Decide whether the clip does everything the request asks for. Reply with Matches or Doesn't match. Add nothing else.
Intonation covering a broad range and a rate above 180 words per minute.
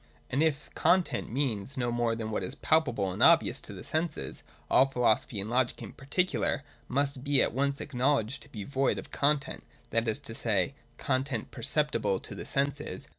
Doesn't match